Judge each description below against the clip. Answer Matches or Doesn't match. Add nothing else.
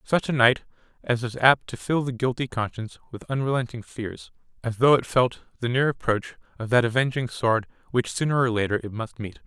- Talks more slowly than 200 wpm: Doesn't match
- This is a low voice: Matches